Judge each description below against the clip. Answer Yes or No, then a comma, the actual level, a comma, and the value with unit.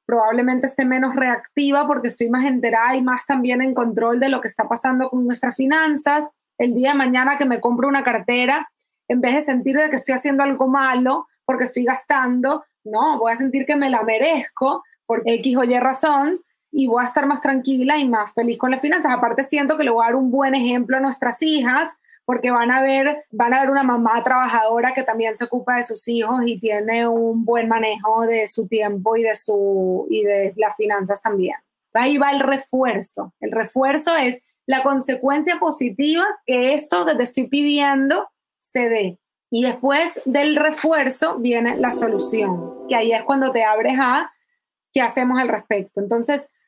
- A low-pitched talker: No, very high, 255 Hz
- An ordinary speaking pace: No, fast, 195 wpm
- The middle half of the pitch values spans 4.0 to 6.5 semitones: No, average, 3.2 semitones